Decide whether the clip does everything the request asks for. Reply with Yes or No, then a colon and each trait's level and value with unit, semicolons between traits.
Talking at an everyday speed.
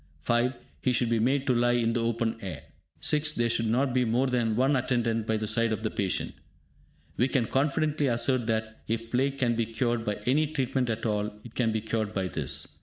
No: fast, 220 wpm